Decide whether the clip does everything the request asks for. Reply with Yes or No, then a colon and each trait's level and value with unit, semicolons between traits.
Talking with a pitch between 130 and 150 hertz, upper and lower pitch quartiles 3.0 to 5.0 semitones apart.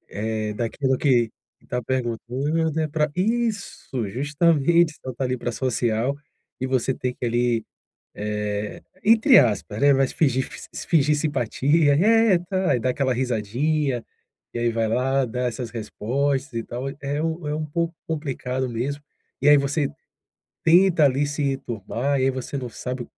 Yes: low, 135 Hz; average, 3.9 semitones